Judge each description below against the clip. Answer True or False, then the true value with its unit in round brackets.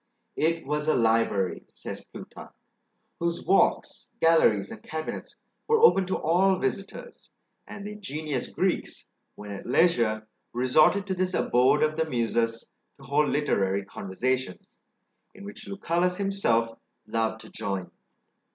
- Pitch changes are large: True (8.1 semitones)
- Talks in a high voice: False (150 Hz)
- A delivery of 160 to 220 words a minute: False (135 wpm)